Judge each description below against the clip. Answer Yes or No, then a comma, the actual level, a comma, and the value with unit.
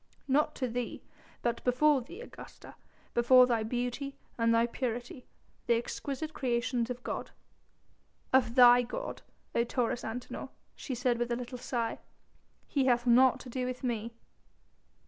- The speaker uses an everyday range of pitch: No, narrow, 1.4 semitones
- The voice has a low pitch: No, high, 245 Hz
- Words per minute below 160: Yes, average, 145 wpm